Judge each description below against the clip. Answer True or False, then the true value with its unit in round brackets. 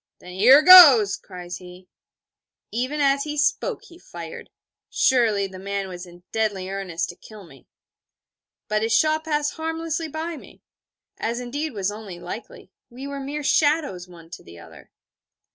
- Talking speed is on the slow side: False (160 wpm)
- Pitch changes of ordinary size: False (8.2 semitones)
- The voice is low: False (225 Hz)